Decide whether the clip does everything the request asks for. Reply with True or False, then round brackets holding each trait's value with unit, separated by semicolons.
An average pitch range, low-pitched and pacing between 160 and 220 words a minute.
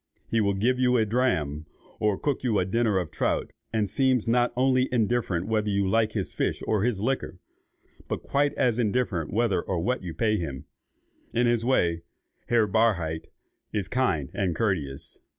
True (4.8 semitones; 110 Hz; 175 wpm)